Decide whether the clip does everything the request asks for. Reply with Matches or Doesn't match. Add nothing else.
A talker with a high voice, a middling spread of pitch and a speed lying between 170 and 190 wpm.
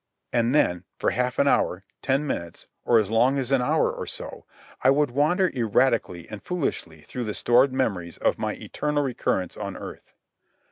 Doesn't match